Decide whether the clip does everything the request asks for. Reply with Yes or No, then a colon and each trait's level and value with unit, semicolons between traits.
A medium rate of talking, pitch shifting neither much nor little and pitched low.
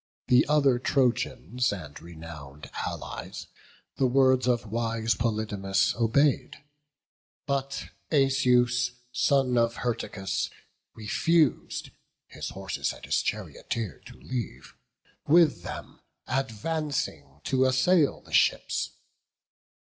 No: slow, 95 wpm; average, 4.6 semitones; low, 125 Hz